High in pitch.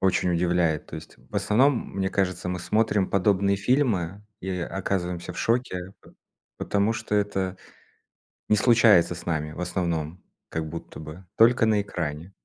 No: very low, 95 Hz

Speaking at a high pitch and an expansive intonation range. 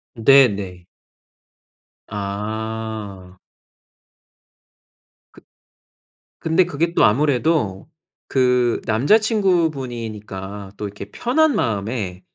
No: low, 110 Hz; wide, 6.3 semitones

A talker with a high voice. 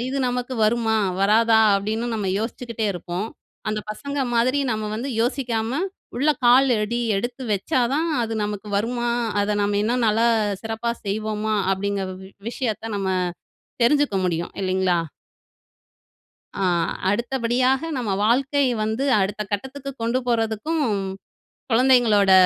Yes: high, 230 Hz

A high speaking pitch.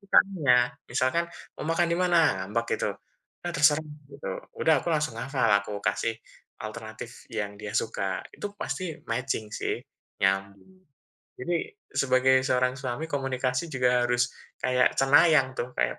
No: low, 130 Hz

